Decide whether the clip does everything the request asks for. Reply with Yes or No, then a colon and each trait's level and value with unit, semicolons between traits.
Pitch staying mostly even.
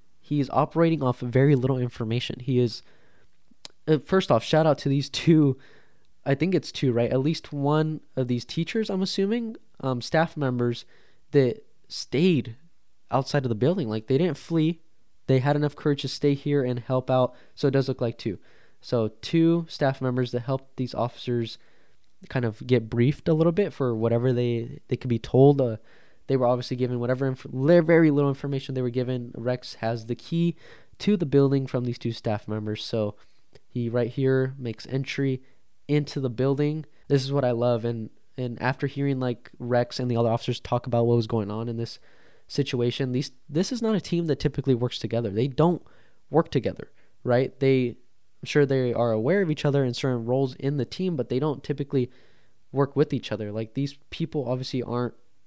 No: average, 3.2 semitones